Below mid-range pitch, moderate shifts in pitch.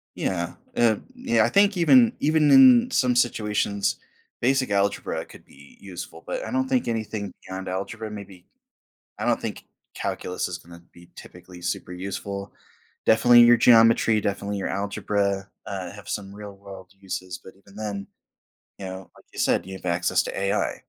Yes: low, 100 Hz; average, 3.9 semitones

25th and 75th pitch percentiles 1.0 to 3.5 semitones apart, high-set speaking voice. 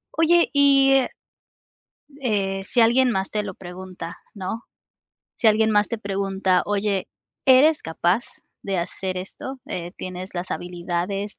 No: average, 4.2 semitones; high, 195 Hz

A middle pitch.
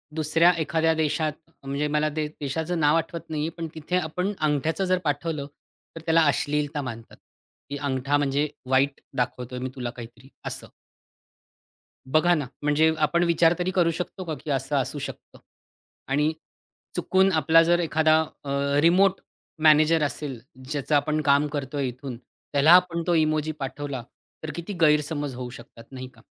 Yes: medium, 150 Hz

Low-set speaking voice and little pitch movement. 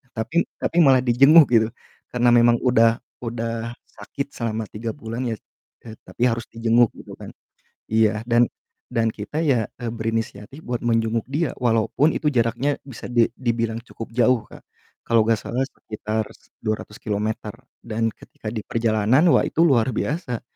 Yes: low, 115 Hz; narrow, 1.8 semitones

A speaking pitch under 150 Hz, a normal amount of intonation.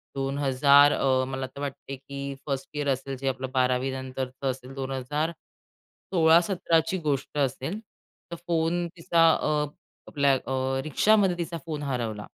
Yes: medium, 140 Hz; average, 3.4 semitones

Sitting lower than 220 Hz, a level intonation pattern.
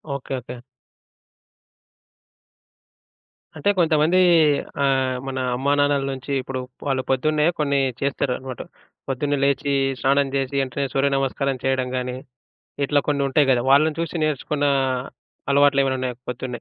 Yes: medium, 140 Hz; narrow, 1.6 semitones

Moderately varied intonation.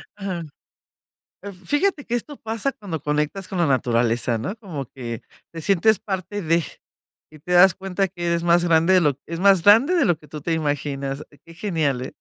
Yes: average, 4.8 semitones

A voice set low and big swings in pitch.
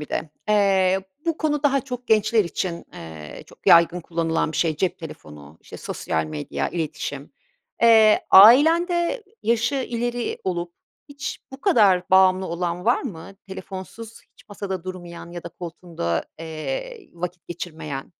No: medium, 185 Hz; wide, 5.8 semitones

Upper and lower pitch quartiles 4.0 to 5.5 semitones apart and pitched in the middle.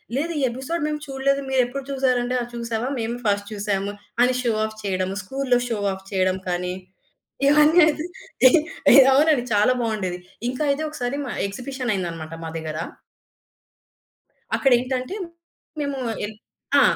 No: average, 5.2 semitones; high, 245 Hz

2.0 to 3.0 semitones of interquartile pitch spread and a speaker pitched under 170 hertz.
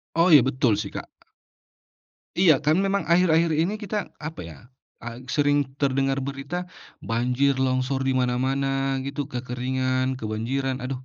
Yes: narrow, 2.4 semitones; low, 135 Hz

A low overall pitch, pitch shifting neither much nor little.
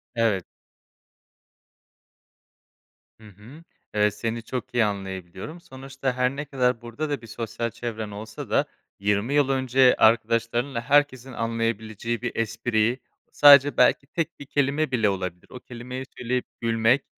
Yes: low, 120 Hz; average, 3.1 semitones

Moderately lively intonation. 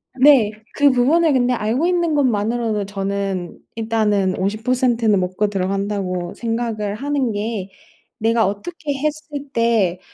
Yes: average, 4.6 semitones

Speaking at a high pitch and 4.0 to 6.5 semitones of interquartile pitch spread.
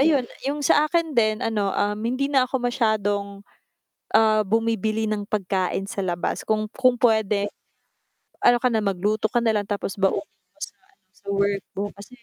No: high, 215 Hz; average, 3.3 semitones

